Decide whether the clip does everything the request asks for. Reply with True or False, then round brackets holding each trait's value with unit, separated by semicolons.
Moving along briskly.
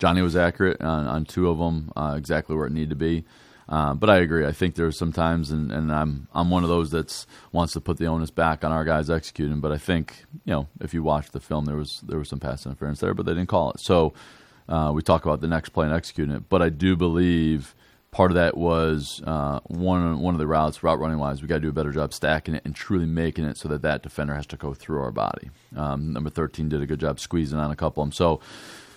True (270 wpm)